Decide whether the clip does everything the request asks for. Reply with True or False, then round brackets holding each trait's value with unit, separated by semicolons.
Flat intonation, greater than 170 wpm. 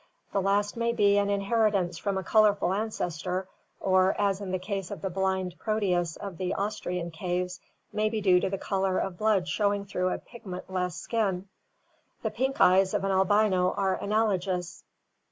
True (2.1 semitones; 180 wpm)